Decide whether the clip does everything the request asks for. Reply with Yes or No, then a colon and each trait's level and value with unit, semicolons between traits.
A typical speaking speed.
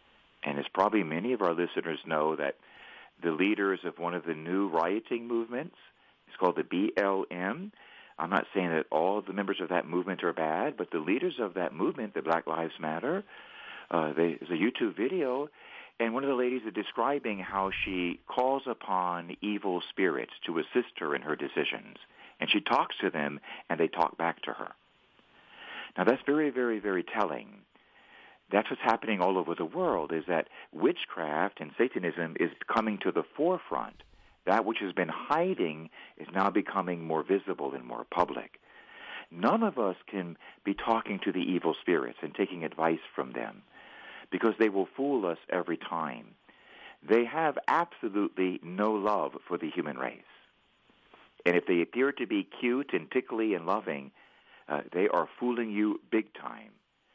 Yes: average, 170 wpm